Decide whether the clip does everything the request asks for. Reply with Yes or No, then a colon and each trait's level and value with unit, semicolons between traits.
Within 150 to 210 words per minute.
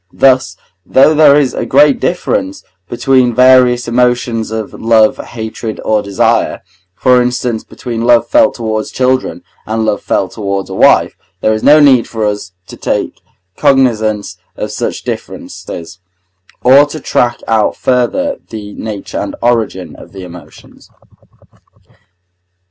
No: slow, 135 wpm